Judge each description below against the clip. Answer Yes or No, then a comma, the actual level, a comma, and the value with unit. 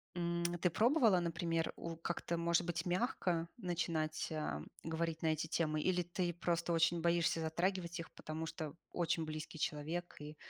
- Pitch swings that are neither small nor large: No, narrow, 1.4 semitones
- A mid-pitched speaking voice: Yes, medium, 170 Hz